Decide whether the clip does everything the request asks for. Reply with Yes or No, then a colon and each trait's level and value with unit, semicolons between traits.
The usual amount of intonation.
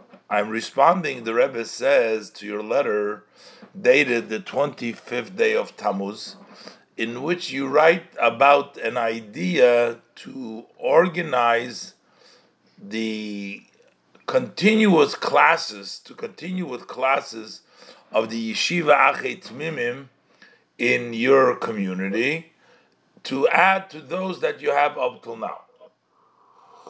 No: wide, 8.6 semitones